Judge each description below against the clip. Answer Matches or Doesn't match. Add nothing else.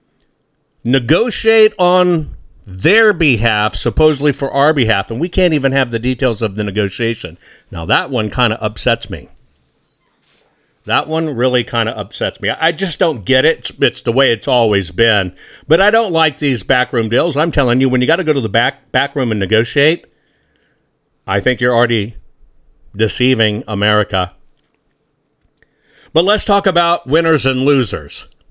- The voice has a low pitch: Matches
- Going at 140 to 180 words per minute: Matches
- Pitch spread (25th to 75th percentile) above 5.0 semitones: Matches